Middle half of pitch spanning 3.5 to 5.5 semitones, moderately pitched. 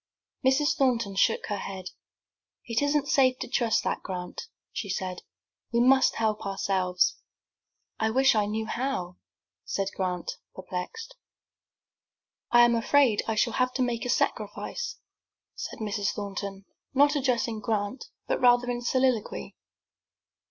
No: average, 4.4 semitones; high, 230 Hz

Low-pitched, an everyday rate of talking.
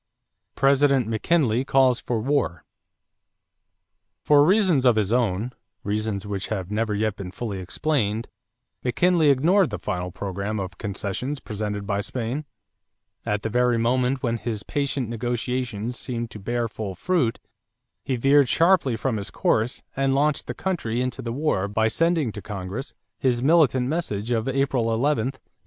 Yes: low, 120 Hz; average, 150 wpm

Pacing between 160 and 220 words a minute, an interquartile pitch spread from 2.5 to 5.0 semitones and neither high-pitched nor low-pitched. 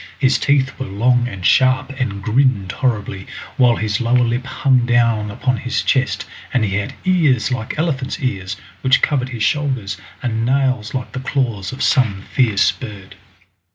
No: average, 165 wpm; average, 3.8 semitones; low, 125 Hz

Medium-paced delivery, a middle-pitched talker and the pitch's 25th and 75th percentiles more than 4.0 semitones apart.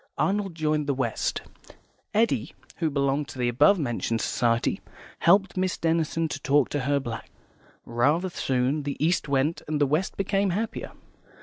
Yes: average, 160 wpm; medium, 150 Hz; average, 4.4 semitones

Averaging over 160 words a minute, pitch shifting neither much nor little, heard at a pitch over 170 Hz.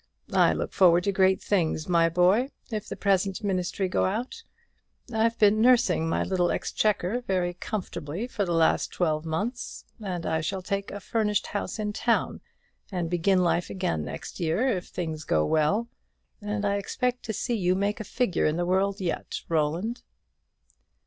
Yes: average, 170 wpm; average, 3.4 semitones; high, 190 Hz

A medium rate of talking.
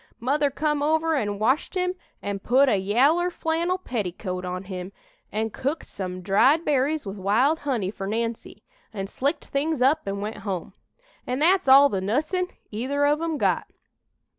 Yes: average, 165 wpm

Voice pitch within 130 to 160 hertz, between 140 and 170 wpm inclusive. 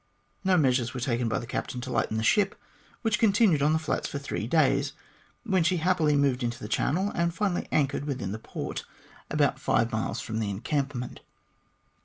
No: medium, 140 Hz; average, 190 wpm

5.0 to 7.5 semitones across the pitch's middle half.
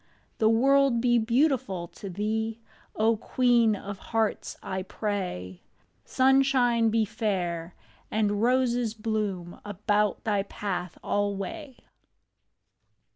No: average, 3.2 semitones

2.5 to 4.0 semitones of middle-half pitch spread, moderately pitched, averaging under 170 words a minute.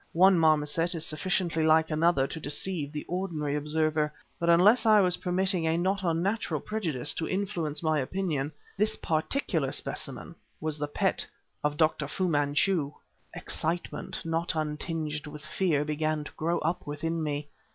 Yes: average, 3.0 semitones; medium, 160 Hz; average, 150 wpm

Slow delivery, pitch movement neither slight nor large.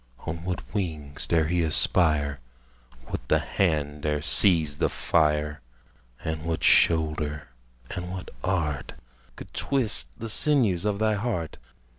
Yes: slow, 130 wpm; average, 3.7 semitones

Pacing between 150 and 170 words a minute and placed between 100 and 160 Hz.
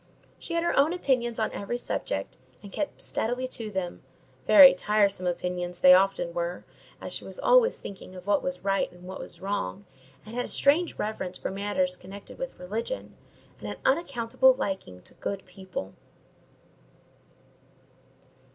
No: average, 155 wpm; high, 200 Hz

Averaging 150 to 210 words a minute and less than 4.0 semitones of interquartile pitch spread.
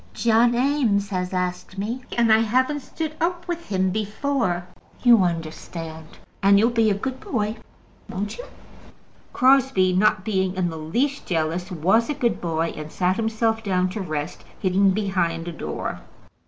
No: average, 160 wpm; average, 4.7 semitones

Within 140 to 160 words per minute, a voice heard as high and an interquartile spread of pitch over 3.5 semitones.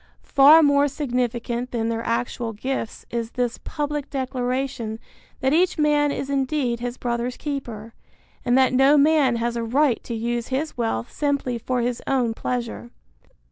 No: average, 155 wpm; very high, 250 Hz; average, 3.0 semitones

